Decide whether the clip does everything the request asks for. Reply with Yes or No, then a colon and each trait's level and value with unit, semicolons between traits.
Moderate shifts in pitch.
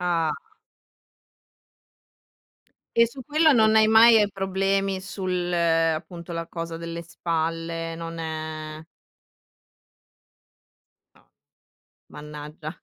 Yes: average, 3.0 semitones